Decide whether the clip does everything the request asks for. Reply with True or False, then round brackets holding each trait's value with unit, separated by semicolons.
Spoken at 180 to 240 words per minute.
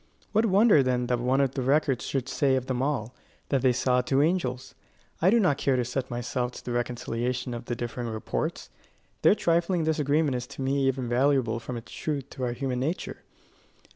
True (200 wpm)